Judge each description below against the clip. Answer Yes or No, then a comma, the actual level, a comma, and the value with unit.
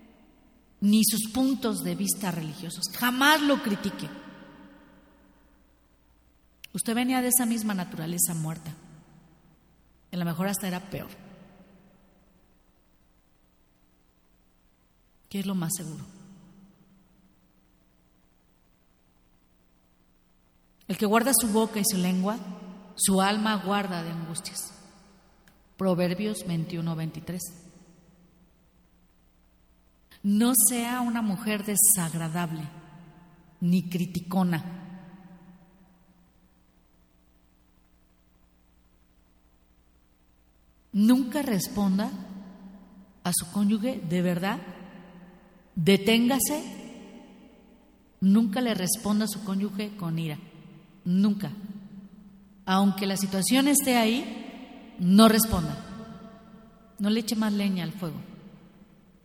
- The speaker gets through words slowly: Yes, slow, 80 wpm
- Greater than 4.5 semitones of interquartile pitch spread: No, average, 4.1 semitones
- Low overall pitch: No, medium, 185 Hz